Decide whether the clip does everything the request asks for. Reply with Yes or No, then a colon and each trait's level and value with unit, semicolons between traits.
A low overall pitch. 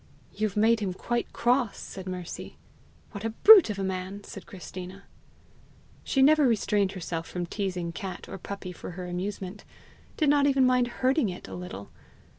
No: high, 200 Hz